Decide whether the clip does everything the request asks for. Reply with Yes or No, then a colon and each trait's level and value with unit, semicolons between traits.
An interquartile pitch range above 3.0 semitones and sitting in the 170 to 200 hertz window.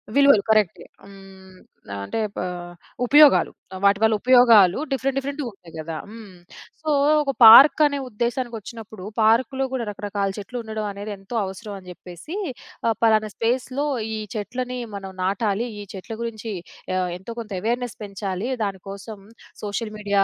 No: average, 3.7 semitones; high, 215 Hz